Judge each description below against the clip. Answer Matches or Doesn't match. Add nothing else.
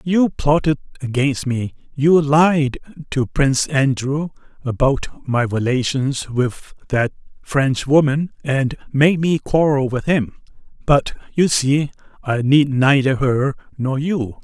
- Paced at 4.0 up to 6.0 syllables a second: Doesn't match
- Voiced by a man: Matches